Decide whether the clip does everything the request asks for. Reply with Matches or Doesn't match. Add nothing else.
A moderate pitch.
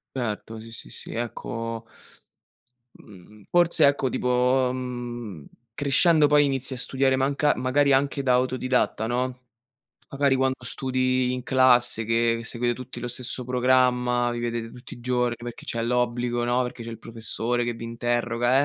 Doesn't match